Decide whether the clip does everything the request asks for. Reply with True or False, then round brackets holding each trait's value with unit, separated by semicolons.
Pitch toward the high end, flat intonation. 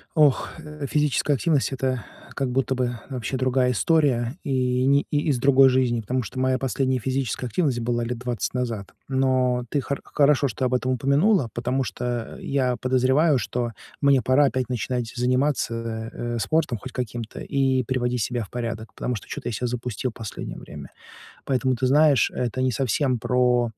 False (130 Hz; 1.9 semitones)